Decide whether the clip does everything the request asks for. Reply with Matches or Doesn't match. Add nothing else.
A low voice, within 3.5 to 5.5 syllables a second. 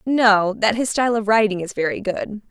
Doesn't match